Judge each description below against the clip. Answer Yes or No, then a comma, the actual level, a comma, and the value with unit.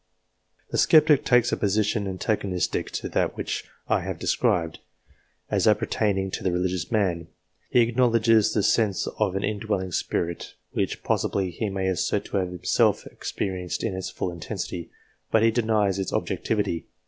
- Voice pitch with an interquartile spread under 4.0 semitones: Yes, average, 3.3 semitones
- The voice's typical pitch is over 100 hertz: No, very low, 95 Hz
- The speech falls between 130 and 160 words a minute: Yes, average, 155 wpm